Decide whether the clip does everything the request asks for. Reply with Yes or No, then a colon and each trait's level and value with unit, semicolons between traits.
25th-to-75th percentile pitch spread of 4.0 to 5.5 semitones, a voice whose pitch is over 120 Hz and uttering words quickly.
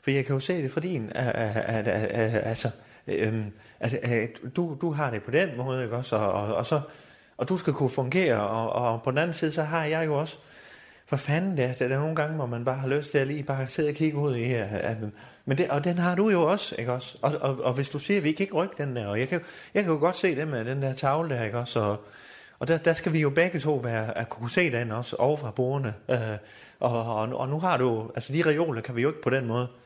Yes: average, 4.9 semitones; low, 135 Hz; fast, 265 wpm